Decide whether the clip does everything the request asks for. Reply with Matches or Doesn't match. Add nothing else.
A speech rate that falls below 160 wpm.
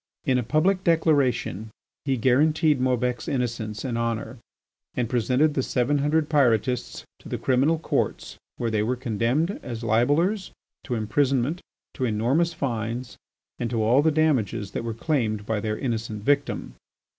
Matches